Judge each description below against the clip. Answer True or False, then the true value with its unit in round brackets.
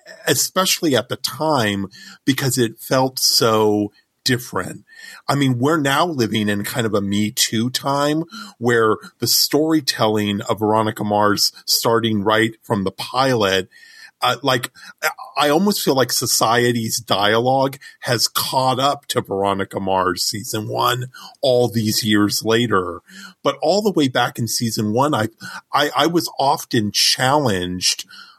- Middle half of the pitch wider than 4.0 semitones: True (4.5 semitones)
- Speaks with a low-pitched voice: True (120 Hz)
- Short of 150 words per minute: True (140 wpm)